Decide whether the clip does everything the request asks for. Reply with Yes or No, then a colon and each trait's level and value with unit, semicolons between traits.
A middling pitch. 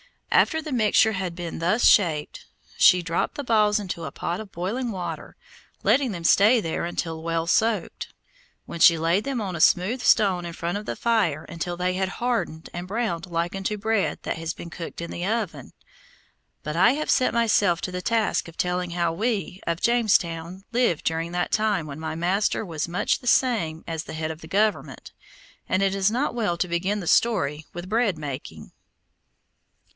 Yes: medium, 180 Hz